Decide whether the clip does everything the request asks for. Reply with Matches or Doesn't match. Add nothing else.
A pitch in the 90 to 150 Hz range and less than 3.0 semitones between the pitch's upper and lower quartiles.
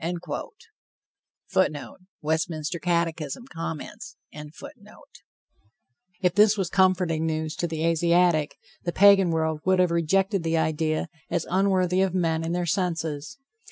Doesn't match